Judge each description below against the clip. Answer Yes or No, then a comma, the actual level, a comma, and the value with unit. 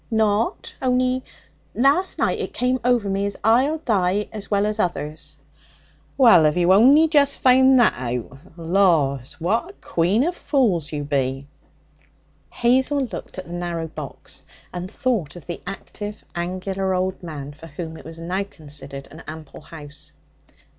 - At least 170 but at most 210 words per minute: No, average, 155 wpm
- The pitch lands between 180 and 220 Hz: Yes, high, 190 Hz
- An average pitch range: No, wide, 7.2 semitones